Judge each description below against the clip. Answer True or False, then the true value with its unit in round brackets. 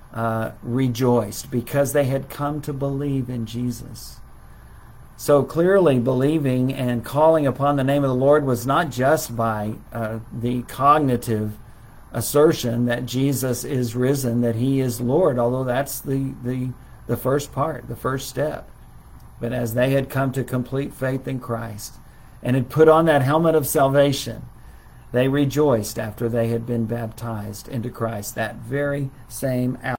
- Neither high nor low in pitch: False (125 Hz)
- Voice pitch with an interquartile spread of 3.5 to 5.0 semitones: False (2.7 semitones)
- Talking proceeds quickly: False (155 wpm)